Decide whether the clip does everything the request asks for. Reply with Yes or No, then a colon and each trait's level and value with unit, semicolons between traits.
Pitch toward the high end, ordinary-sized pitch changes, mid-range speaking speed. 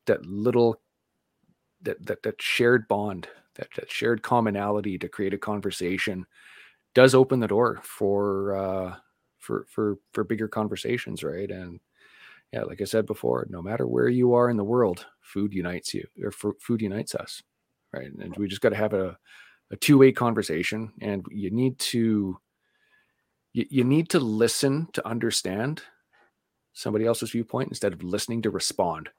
No: low, 105 Hz; average, 3.1 semitones; average, 160 wpm